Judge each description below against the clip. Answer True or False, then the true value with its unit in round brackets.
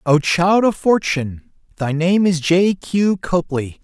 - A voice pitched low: False (175 Hz)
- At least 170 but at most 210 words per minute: False (155 wpm)